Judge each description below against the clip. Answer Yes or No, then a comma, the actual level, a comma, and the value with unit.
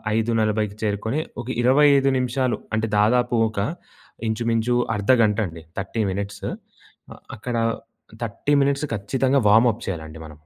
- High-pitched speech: No, low, 115 Hz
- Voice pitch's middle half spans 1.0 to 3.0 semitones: No, average, 3.6 semitones